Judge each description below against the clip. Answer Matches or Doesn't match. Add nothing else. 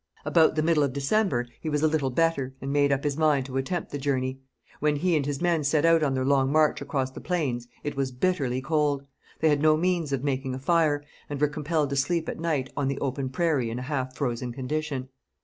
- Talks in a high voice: Doesn't match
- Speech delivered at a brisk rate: Matches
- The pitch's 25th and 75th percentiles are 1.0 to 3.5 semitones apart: Matches